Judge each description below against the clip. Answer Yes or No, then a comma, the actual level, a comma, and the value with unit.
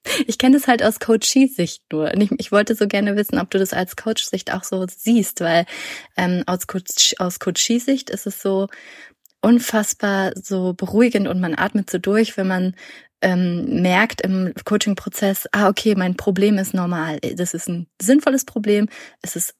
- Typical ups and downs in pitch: Yes, average, 3.2 semitones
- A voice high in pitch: Yes, high, 200 Hz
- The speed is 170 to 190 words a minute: Yes, average, 185 wpm